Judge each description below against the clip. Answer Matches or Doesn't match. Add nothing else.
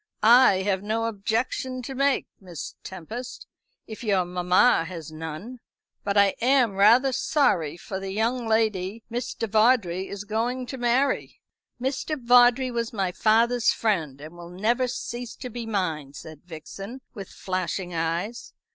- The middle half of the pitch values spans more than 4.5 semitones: Matches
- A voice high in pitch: Matches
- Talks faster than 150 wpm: Doesn't match